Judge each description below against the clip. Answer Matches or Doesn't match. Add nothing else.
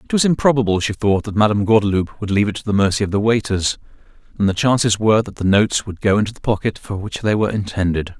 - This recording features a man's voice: Matches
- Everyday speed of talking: Doesn't match